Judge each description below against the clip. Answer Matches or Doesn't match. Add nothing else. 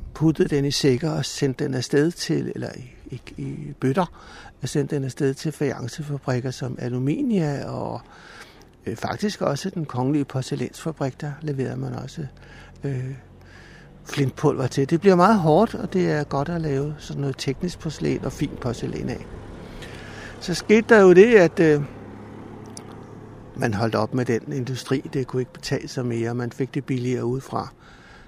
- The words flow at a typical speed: Matches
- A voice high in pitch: Doesn't match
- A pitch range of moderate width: Matches